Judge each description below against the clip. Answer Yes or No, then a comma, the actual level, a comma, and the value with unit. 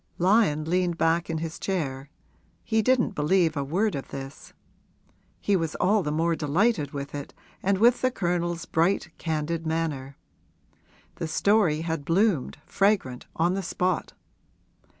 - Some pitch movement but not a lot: Yes, average, 4.3 semitones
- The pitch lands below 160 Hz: No, medium, 165 Hz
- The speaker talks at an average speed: Yes, average, 145 wpm